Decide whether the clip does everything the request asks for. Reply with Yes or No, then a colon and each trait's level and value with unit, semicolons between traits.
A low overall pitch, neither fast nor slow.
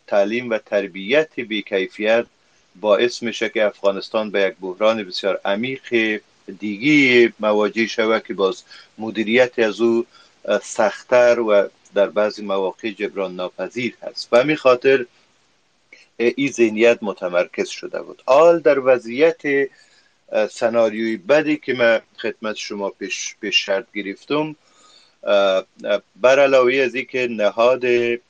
Yes: low, 115 Hz; average, 120 wpm